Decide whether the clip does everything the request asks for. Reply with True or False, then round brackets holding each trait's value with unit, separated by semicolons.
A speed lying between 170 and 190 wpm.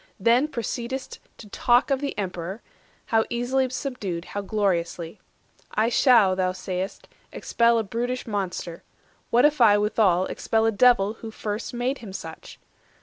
False (145 wpm)